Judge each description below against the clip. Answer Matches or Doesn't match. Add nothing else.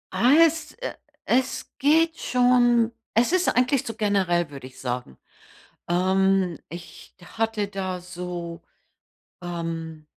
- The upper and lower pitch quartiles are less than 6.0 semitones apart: Doesn't match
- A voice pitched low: Doesn't match